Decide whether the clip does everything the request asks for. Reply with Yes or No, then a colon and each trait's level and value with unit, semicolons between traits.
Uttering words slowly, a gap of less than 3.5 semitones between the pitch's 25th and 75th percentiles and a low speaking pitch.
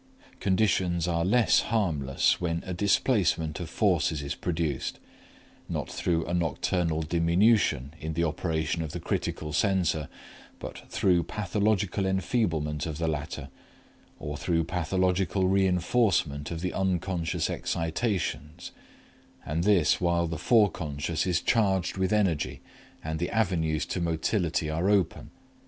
Yes: slow, 125 wpm; average, 3.1 semitones; very low, 85 Hz